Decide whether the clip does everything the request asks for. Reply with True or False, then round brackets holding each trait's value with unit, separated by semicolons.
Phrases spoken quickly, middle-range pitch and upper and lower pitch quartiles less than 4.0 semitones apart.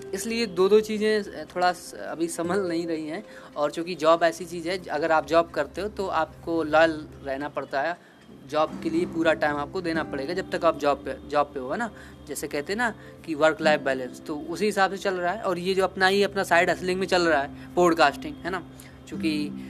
True (230 wpm; 165 Hz; 3.5 semitones)